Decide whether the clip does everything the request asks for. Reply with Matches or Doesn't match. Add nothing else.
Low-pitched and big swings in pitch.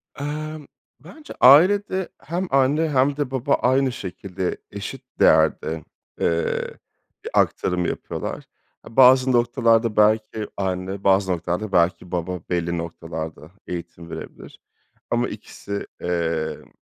Matches